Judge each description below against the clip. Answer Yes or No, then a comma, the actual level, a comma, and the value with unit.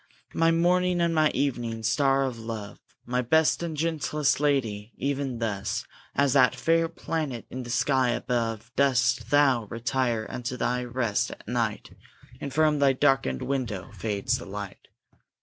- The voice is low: Yes, low, 130 Hz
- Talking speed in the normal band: Yes, average, 150 wpm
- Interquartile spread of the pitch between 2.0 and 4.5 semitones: Yes, average, 3.8 semitones